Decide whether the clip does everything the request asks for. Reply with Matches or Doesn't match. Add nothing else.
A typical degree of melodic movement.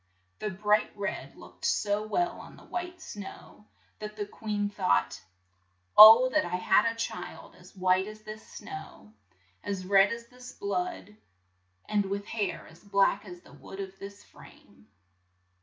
Doesn't match